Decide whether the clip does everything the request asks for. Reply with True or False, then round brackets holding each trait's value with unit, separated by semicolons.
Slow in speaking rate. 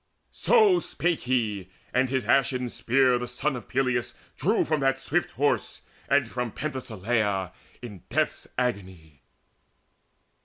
True (125 wpm)